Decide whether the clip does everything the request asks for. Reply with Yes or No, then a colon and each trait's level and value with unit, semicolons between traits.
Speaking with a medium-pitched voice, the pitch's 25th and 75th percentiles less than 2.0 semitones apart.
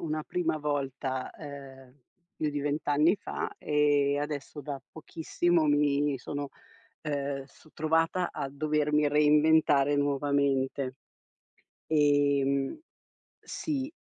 Yes: medium, 145 Hz; narrow, 1.5 semitones